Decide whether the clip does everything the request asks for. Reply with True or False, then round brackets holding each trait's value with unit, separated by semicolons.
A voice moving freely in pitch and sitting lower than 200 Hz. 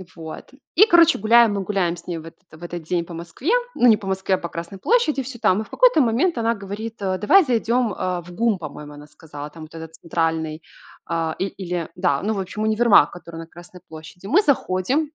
True (5.7 semitones; 185 Hz)